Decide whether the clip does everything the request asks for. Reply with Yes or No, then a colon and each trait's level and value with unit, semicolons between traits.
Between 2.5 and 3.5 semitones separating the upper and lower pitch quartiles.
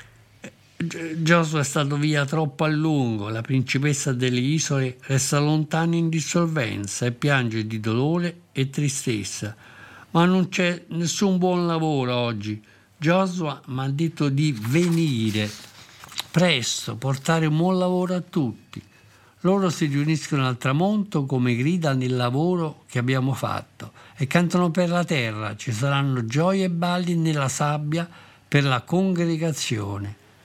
No: average, 5.2 semitones